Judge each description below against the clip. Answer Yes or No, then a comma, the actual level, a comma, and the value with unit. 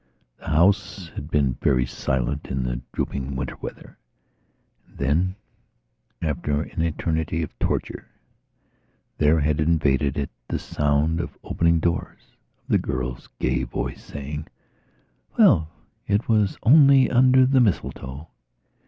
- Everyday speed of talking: No, slow, 125 wpm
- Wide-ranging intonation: No, average, 3.8 semitones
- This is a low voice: Yes, very low, 75 Hz